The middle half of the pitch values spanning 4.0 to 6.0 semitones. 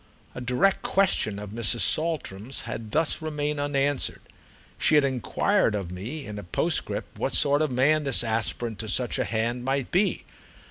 Yes: average, 5.1 semitones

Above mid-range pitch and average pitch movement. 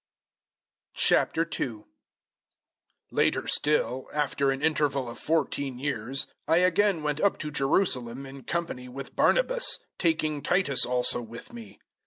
No: medium, 145 Hz; average, 4.2 semitones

